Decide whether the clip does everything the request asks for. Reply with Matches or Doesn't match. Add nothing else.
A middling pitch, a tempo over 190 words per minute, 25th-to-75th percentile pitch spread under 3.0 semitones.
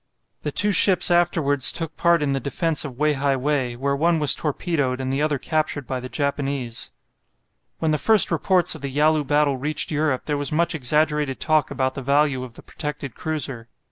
Matches